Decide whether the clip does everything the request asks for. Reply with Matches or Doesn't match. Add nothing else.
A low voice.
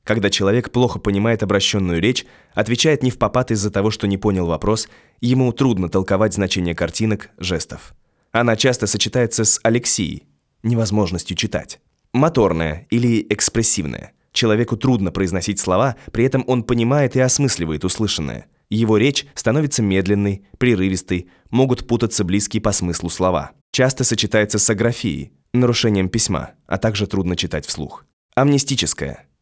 Matches